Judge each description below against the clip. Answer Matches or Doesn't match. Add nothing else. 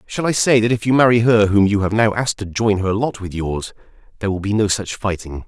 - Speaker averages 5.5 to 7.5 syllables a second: Matches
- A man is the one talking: Matches